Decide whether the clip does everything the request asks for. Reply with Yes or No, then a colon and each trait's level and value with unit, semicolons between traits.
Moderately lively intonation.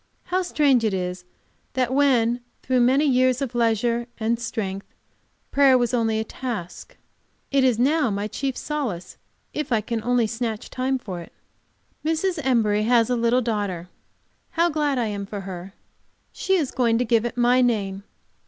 Yes: average, 3.4 semitones